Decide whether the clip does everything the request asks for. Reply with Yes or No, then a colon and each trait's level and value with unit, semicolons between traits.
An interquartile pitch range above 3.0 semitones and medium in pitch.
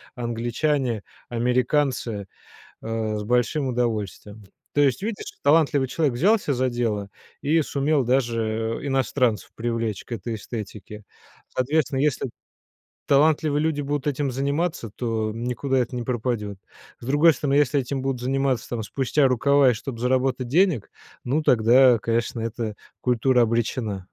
No: average, 3.5 semitones; low, 125 Hz